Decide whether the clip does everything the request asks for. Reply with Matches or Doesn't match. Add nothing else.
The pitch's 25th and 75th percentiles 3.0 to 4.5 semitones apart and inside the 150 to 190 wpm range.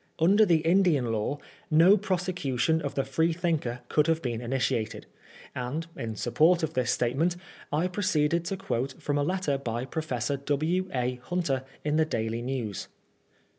Doesn't match